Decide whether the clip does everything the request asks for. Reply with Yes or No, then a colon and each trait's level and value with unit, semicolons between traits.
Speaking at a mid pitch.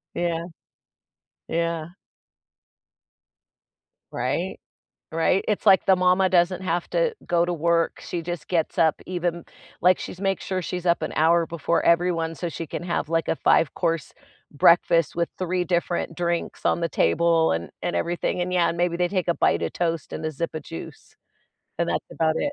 Yes: medium, 170 Hz